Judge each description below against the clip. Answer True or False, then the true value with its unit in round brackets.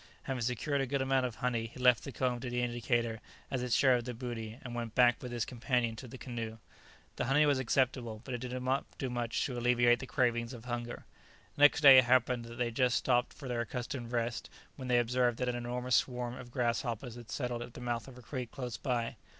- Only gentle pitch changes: True (1.3 semitones)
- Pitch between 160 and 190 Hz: False (125 Hz)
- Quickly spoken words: True (240 wpm)